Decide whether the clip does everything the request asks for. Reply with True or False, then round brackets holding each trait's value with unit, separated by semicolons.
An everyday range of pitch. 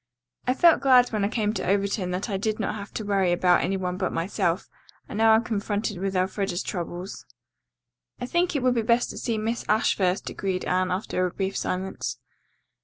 True (3.1 semitones)